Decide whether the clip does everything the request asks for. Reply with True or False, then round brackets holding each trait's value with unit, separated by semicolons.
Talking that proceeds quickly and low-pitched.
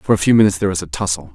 True (355 wpm; 95 Hz)